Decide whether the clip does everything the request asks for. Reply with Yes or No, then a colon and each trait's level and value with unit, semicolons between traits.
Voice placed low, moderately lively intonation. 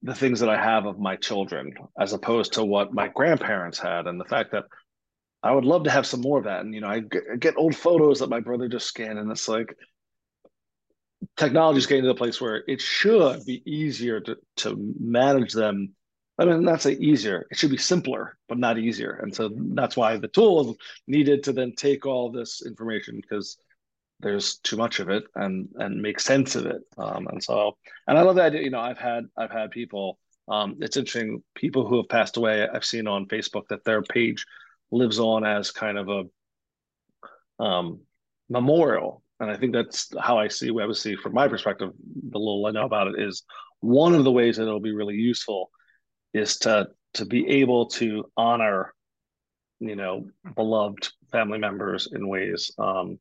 Yes: low, 115 Hz; average, 3.3 semitones